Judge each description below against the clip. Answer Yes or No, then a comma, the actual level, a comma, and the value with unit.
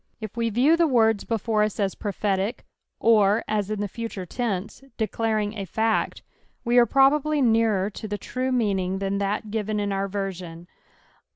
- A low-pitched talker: No, high, 215 Hz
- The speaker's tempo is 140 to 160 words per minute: No, average, 170 wpm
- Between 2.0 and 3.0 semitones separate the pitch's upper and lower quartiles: Yes, narrow, 2.6 semitones